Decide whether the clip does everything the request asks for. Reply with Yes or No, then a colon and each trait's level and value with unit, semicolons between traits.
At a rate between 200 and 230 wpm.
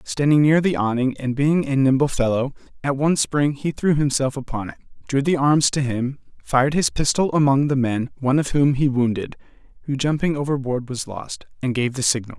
Yes: fast, 205 wpm